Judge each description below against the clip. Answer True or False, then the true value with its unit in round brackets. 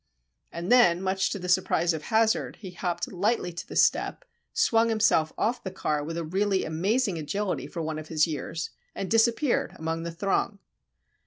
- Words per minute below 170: False (180 wpm)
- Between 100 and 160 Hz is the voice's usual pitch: False (185 Hz)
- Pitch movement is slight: False (4.4 semitones)